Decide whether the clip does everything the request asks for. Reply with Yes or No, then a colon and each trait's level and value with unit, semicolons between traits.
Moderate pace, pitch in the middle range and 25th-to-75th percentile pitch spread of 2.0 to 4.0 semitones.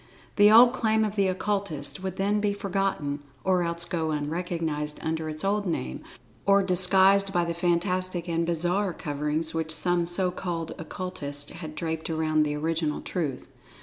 Yes: average, 160 wpm; medium, 175 Hz; average, 3.4 semitones